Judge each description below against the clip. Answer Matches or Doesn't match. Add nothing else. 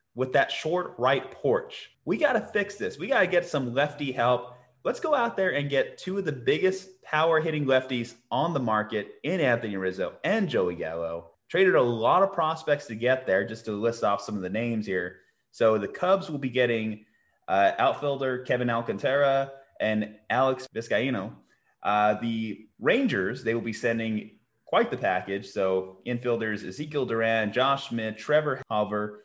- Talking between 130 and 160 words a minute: Doesn't match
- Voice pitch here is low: Matches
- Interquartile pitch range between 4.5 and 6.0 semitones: Matches